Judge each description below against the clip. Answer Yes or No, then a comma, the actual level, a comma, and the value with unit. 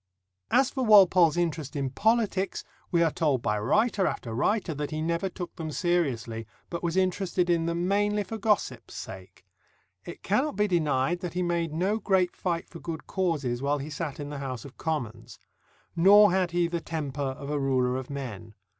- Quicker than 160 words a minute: Yes, average, 190 wpm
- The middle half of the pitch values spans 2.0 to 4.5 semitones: No, average, 5.0 semitones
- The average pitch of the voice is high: No, medium, 170 Hz